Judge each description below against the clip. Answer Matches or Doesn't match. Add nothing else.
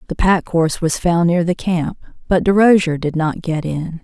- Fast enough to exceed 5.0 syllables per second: Doesn't match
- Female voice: Matches